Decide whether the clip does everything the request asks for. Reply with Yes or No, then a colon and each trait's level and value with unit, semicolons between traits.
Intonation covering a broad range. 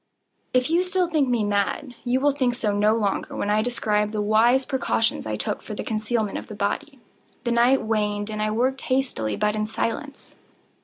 No: average, 3.7 semitones